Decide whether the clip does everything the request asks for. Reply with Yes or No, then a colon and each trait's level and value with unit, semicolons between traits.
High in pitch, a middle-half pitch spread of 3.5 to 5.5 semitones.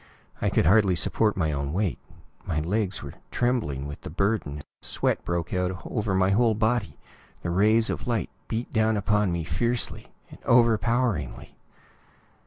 No: low, 100 Hz; average, 4.7 semitones